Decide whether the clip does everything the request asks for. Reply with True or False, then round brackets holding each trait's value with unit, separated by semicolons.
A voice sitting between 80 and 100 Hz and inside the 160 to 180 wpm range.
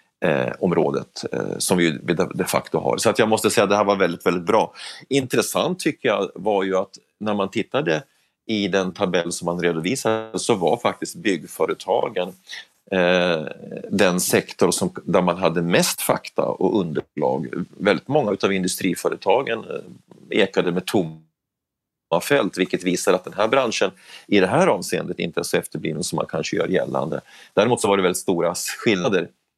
True (95 Hz; 170 wpm)